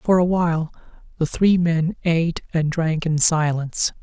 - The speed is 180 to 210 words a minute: No, average, 165 wpm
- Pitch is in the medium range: Yes, medium, 165 Hz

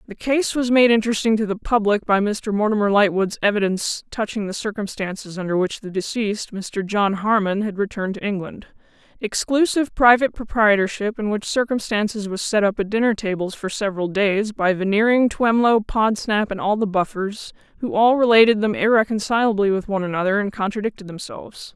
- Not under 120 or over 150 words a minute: No, average, 170 wpm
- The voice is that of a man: No, female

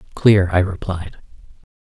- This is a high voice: No, very low, 95 Hz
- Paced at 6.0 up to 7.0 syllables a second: No, 4.4 syllables/s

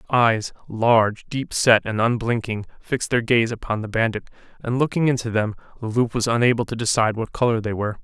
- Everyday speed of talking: Yes, average, 195 wpm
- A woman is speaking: No, male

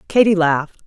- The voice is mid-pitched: Yes, medium, 180 Hz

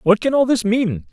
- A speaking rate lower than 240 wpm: No, fast, 270 wpm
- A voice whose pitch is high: Yes, high, 215 Hz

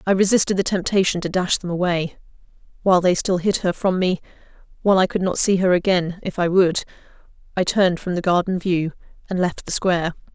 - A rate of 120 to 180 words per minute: No, average, 190 wpm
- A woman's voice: Yes, female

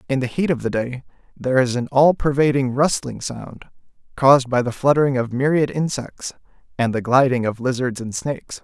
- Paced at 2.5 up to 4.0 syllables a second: No, 5.4 syllables/s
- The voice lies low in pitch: Yes, low, 130 Hz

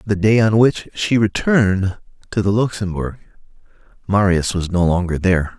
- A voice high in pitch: No, low, 100 Hz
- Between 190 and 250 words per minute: No, average, 150 wpm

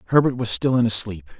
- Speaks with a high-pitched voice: No, low, 115 Hz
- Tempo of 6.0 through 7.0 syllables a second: Yes, 6.5 syllables/s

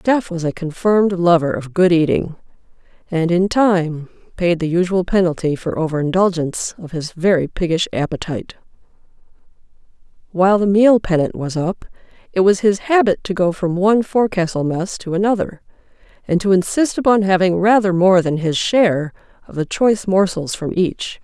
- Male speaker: No, female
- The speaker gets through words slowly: No, average, 165 wpm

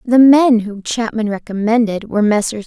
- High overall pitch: Yes, high, 225 Hz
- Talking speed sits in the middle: Yes, average, 160 wpm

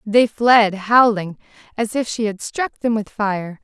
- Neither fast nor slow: Yes, average, 180 wpm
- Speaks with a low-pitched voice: No, high, 220 Hz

